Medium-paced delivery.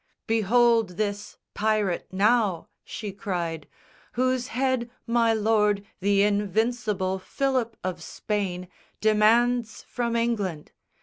No: slow, 100 wpm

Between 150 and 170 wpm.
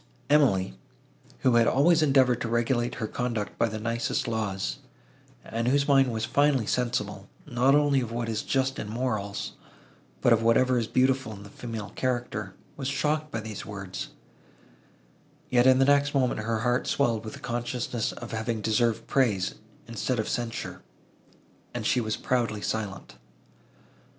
Yes: average, 160 wpm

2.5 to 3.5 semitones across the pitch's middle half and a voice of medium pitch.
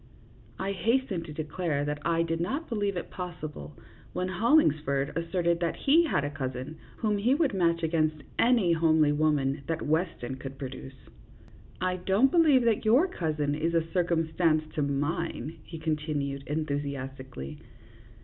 No: average, 4.1 semitones; medium, 165 Hz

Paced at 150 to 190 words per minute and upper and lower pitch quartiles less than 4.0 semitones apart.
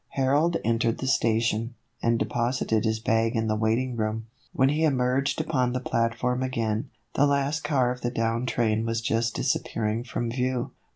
Yes: average, 170 wpm; narrow, 2.4 semitones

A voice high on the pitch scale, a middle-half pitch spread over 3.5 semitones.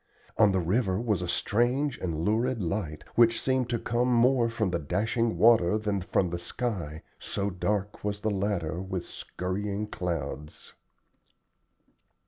No: low, 100 Hz; average, 4.4 semitones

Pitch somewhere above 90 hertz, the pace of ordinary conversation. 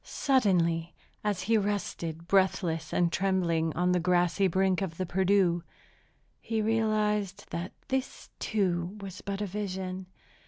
No: high, 190 Hz; slow, 130 wpm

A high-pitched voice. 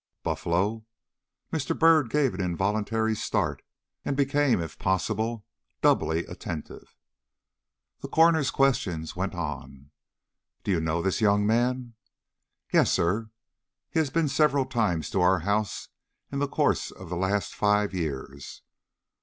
No: low, 105 Hz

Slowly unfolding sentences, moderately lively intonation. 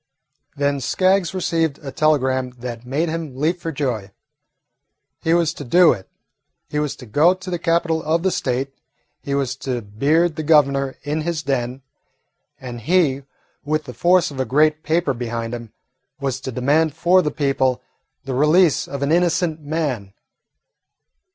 No: average, 165 wpm; average, 4.0 semitones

